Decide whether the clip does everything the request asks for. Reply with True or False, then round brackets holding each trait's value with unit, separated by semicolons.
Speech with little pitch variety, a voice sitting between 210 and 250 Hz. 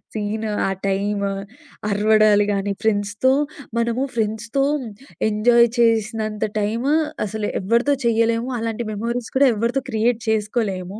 True (2.0 semitones; 220 Hz)